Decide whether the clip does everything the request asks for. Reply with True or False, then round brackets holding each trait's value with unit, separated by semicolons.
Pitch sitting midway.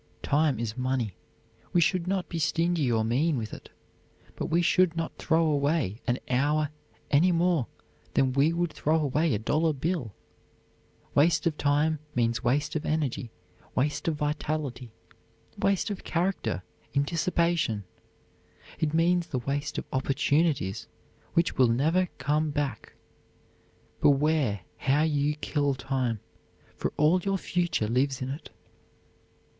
True (150 Hz)